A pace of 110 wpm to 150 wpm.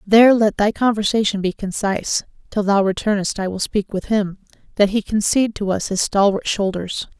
No: average, 185 wpm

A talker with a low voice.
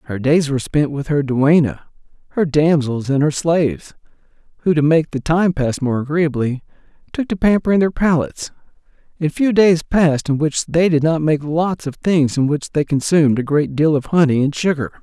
No: medium, 150 Hz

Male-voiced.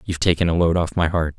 Yes: male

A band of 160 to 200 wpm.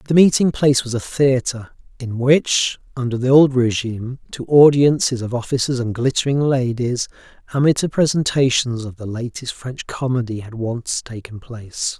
No: average, 150 wpm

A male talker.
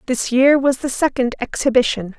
No: female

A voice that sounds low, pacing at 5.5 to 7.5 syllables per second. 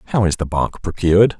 Yes: very low, 95 Hz; 6.2 syllables/s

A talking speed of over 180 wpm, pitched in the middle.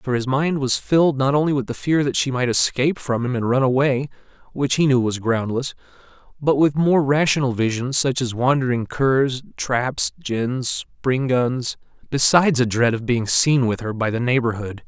No: average, 195 wpm; low, 130 Hz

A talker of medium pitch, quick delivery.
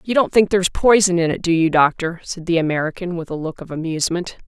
Yes: medium, 175 Hz; fast, 240 wpm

